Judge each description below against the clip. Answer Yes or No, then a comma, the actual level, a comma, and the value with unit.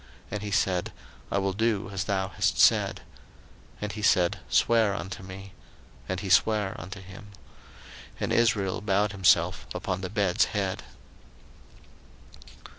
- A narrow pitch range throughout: Yes, narrow, 1.9 semitones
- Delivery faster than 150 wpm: No, average, 140 wpm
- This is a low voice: Yes, very low, 95 Hz